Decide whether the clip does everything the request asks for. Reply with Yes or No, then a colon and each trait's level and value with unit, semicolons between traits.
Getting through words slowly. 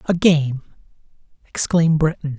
Yes: slow, 100 wpm